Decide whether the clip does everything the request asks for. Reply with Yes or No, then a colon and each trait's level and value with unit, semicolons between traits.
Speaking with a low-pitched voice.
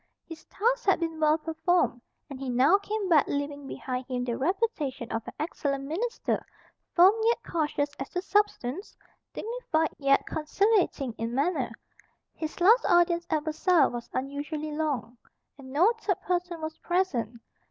No: very high, 315 Hz